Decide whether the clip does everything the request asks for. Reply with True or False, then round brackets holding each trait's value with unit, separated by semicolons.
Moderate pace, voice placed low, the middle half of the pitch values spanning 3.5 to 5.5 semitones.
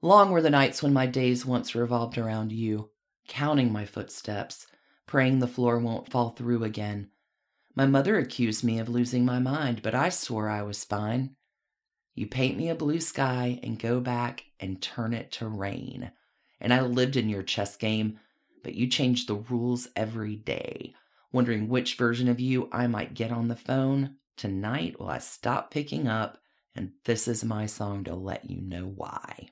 False (185 wpm; 120 Hz; 2.9 semitones)